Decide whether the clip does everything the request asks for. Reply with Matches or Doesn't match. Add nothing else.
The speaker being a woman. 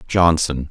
Doesn't match